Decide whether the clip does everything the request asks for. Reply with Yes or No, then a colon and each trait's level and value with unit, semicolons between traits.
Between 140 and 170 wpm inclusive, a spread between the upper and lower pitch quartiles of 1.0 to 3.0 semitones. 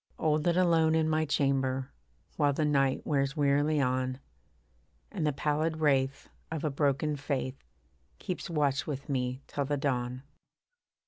Yes: average, 145 wpm; narrow, 2.4 semitones